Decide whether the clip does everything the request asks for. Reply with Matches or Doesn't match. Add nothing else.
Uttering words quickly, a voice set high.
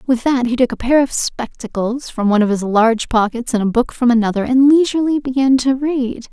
Matches